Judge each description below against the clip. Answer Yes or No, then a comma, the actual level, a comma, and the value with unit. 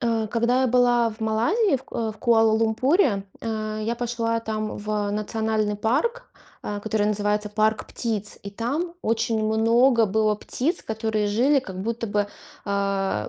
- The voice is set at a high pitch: Yes, high, 220 Hz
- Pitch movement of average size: No, narrow, 2.0 semitones